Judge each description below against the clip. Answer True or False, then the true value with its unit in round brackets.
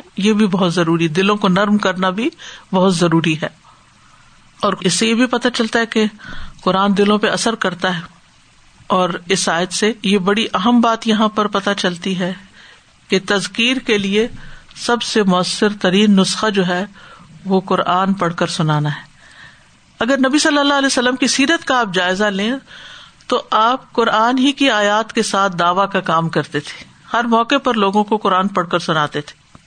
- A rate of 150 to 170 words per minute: False (185 wpm)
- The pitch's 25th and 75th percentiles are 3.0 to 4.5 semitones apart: True (3.7 semitones)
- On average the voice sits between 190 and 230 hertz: True (200 Hz)